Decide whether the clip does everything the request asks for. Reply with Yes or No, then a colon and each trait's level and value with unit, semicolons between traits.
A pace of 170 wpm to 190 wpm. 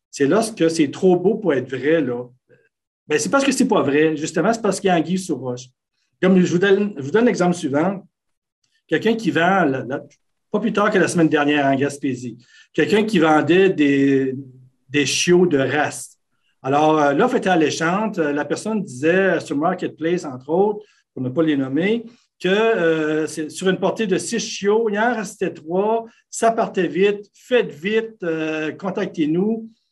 Yes: average, 180 wpm